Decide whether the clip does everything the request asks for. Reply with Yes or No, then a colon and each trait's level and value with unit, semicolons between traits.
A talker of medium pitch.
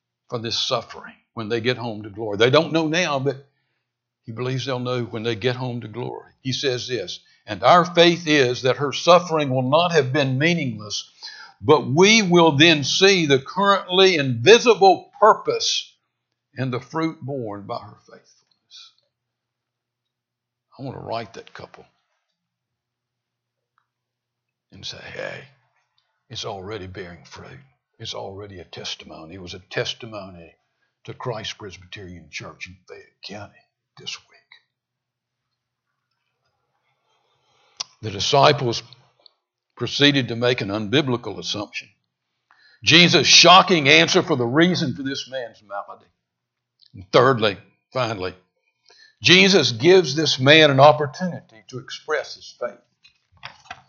No: low, 130 Hz